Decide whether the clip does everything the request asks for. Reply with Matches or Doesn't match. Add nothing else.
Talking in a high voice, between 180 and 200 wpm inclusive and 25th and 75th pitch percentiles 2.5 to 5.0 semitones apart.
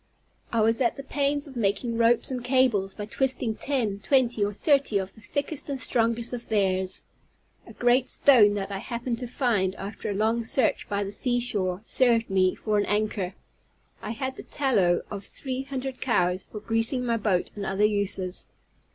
Matches